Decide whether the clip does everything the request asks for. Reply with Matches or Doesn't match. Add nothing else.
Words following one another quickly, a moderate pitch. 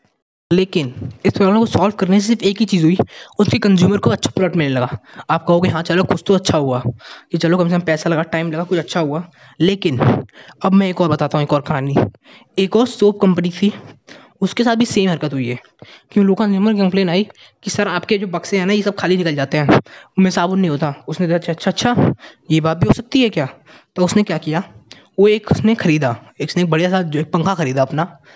Matches